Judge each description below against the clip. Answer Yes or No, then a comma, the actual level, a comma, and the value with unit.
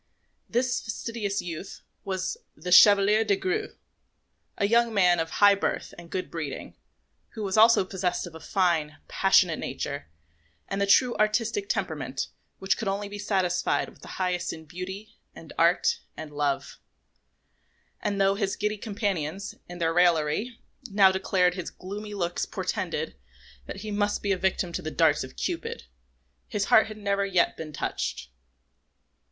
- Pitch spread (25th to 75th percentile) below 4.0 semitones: Yes, average, 3.0 semitones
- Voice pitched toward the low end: No, high, 195 Hz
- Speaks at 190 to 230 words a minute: No, average, 160 wpm